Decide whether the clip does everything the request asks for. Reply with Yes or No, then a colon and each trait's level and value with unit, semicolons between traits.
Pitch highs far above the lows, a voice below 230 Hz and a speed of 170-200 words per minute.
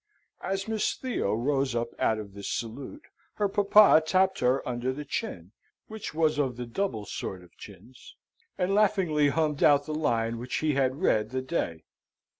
Yes: wide, 7.5 semitones; medium, 140 Hz; average, 175 wpm